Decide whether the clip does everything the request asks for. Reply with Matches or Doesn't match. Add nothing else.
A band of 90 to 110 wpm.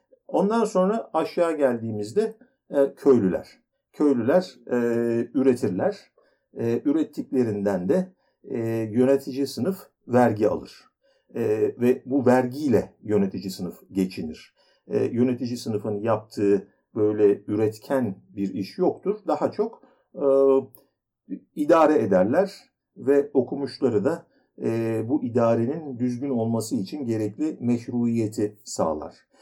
Matches